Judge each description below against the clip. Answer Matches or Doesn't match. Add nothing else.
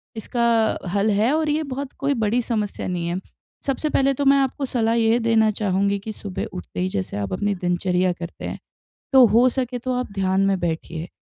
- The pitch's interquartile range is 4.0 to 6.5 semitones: Matches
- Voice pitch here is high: Matches